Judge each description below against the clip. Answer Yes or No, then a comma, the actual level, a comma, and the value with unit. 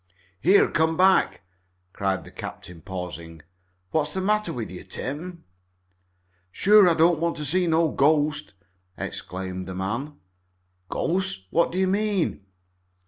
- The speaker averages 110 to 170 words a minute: Yes, slow, 135 wpm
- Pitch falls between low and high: Yes, medium, 155 Hz